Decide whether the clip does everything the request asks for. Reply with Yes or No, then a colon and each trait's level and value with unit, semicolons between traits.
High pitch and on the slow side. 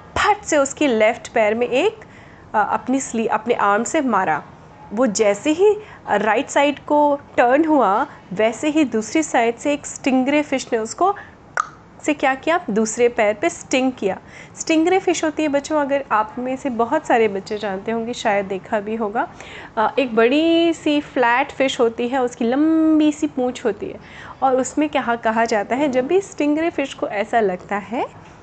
No: very high, 260 Hz; average, 175 wpm